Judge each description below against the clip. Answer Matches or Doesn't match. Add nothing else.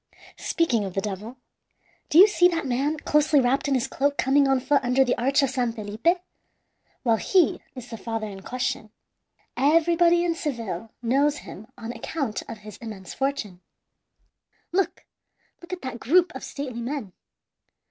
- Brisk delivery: Doesn't match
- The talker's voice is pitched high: Matches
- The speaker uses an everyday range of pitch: Matches